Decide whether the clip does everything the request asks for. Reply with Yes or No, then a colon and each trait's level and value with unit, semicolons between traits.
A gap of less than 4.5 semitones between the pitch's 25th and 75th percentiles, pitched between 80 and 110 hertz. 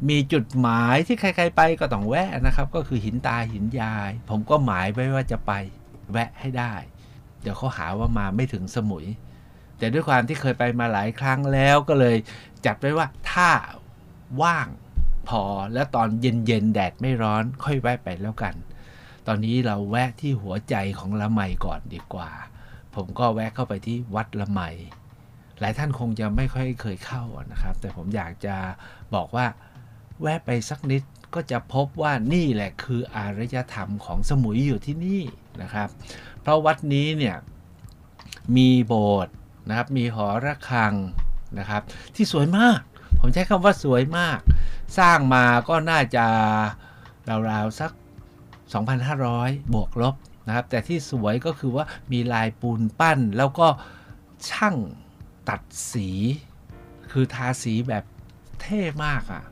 No: average, 4.0 semitones; low, 120 Hz